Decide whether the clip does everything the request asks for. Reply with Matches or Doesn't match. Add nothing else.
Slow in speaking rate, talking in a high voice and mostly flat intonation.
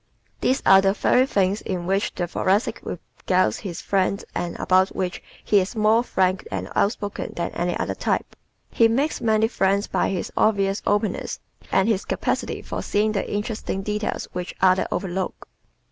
Doesn't match